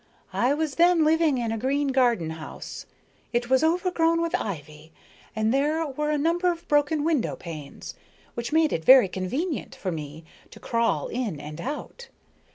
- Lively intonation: Yes, wide, 8.8 semitones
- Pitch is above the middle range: Yes, very high, 265 Hz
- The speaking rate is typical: Yes, average, 165 wpm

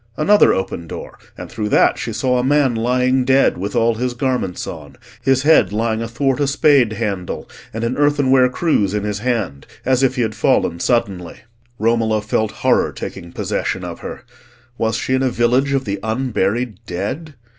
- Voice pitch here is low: Yes, low, 120 Hz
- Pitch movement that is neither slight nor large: Yes, average, 3.8 semitones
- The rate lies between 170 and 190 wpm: Yes, average, 180 wpm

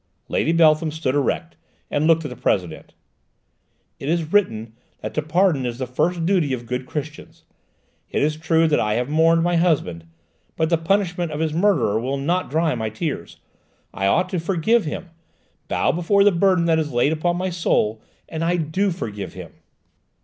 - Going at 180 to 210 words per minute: Yes, average, 185 wpm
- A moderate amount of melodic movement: Yes, average, 4.8 semitones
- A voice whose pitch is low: No, medium, 160 Hz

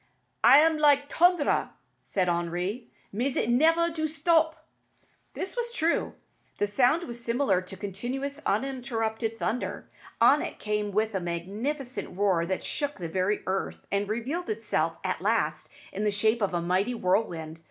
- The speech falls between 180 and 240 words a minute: No, average, 155 wpm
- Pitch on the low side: No, high, 220 Hz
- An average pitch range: No, wide, 6.7 semitones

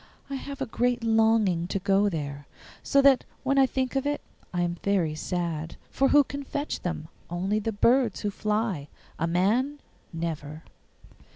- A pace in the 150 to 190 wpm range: Yes, average, 170 wpm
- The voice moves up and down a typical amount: No, wide, 7.2 semitones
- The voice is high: Yes, high, 205 Hz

